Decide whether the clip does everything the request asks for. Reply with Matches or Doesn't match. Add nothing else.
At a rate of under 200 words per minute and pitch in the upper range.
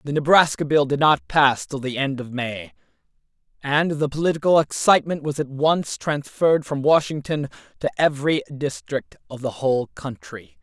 Doesn't match